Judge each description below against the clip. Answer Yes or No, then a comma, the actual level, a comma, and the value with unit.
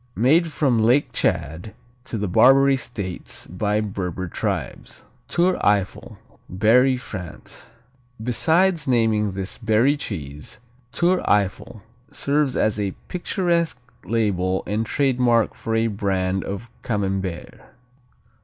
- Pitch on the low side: Yes, low, 110 Hz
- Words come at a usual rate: No, slow, 110 wpm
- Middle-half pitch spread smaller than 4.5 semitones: No, average, 5.3 semitones